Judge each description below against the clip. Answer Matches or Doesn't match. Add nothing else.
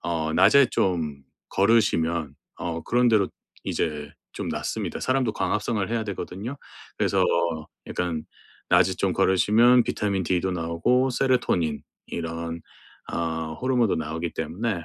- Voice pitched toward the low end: Matches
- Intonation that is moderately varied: Doesn't match